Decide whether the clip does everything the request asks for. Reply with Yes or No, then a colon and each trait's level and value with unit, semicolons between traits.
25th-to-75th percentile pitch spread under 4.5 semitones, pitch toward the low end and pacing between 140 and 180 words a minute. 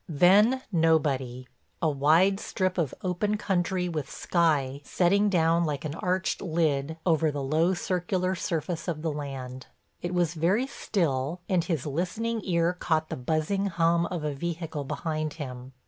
No: average, 3.3 semitones; medium, 165 Hz; average, 155 wpm